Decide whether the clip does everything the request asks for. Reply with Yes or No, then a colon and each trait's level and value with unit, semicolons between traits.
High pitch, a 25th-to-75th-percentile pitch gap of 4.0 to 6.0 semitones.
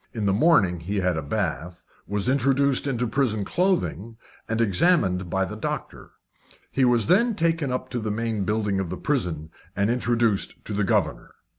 No: low, 110 Hz; wide, 5.5 semitones